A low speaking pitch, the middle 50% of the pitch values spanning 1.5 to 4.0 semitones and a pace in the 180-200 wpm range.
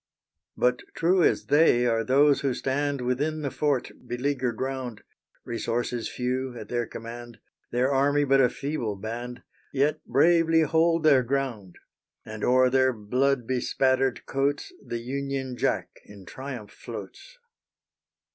No: low, 130 Hz; average, 2.8 semitones; slow, 135 wpm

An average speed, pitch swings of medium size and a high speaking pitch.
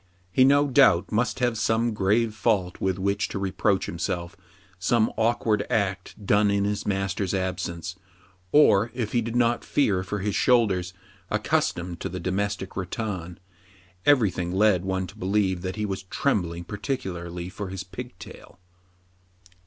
No: average, 150 wpm; average, 3.2 semitones; low, 100 Hz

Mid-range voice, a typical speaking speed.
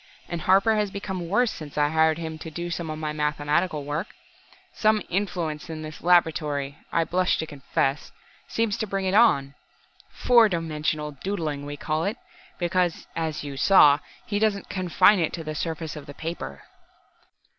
Yes: medium, 165 Hz; average, 170 wpm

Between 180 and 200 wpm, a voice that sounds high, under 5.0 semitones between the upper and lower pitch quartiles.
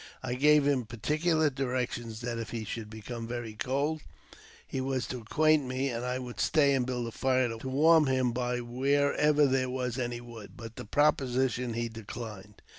No: average, 190 wpm; low, 125 Hz; average, 2.7 semitones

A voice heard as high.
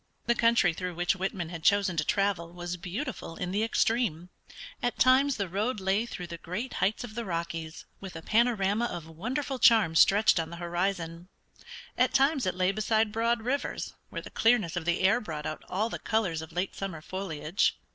Yes: high, 195 Hz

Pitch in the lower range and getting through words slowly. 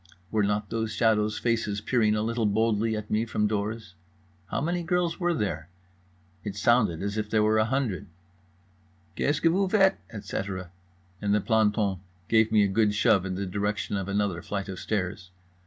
No: low, 105 Hz; average, 180 wpm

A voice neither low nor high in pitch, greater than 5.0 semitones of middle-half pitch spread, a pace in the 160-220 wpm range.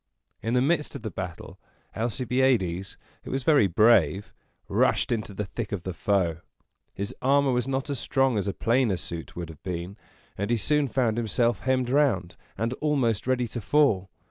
No: low, 115 Hz; wide, 5.4 semitones; average, 180 wpm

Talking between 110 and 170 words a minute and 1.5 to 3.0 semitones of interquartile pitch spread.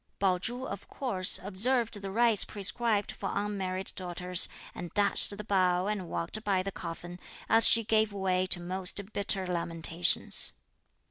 Yes: average, 150 wpm; narrow, 2.5 semitones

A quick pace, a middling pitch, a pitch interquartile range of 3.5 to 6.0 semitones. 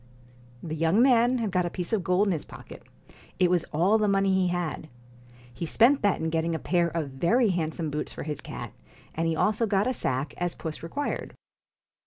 Yes: fast, 210 wpm; medium, 175 Hz; average, 4.3 semitones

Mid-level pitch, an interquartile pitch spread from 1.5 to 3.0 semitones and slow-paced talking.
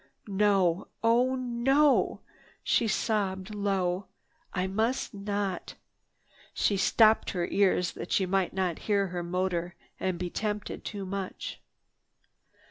No: high, 195 Hz; narrow, 2.6 semitones; slow, 120 wpm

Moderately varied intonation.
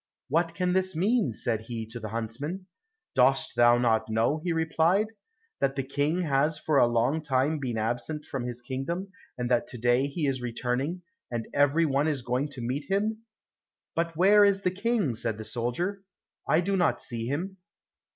No: wide, 6.1 semitones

